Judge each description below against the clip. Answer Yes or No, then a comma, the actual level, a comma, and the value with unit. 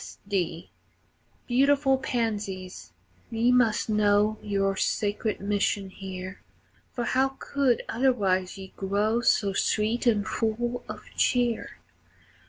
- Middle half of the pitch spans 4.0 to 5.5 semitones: No, average, 3.5 semitones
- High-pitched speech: Yes, high, 215 Hz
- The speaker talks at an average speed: No, slow, 110 wpm